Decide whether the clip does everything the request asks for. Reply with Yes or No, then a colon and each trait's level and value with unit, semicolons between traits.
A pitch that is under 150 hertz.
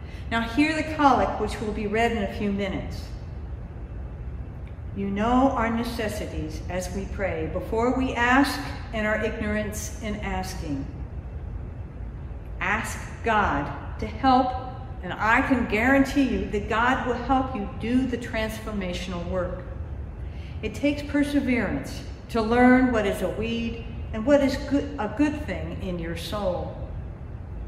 No: high, 235 Hz